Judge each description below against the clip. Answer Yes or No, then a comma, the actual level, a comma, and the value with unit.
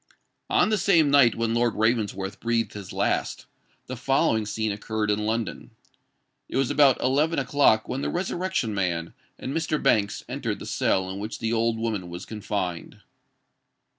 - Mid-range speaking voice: No, low, 115 Hz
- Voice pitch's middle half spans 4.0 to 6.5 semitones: Yes, average, 4.5 semitones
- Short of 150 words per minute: No, average, 165 wpm